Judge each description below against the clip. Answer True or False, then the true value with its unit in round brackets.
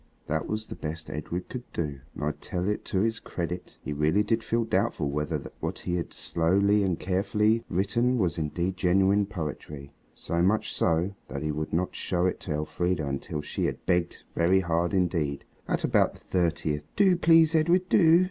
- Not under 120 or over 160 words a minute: False (190 wpm)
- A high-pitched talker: False (90 Hz)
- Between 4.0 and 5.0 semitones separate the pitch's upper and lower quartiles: True (4.7 semitones)